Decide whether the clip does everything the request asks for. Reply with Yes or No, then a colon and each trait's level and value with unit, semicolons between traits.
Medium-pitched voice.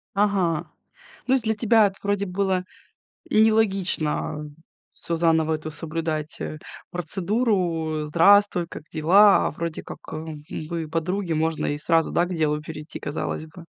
Yes: medium, 170 Hz